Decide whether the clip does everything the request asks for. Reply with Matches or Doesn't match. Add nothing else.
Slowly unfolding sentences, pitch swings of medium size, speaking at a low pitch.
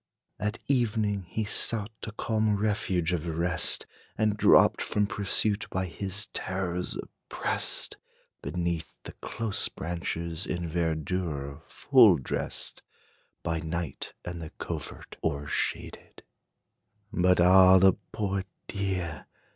Matches